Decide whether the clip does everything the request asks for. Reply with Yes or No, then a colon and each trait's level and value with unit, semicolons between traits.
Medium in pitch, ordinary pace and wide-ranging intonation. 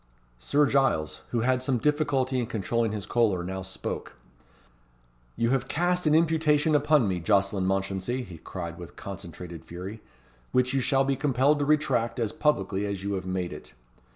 No: low, 115 Hz; average, 170 wpm; wide, 6.4 semitones